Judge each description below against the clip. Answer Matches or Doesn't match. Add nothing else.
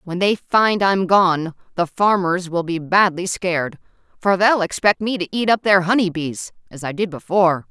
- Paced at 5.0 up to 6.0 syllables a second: Doesn't match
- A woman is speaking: Matches